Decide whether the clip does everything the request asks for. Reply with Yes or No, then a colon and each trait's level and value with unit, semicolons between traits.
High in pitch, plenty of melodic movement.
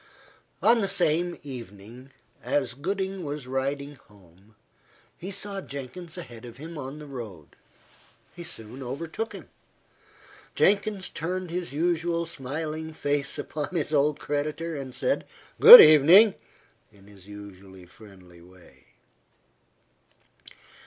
No: medium, 145 Hz; wide, 6.4 semitones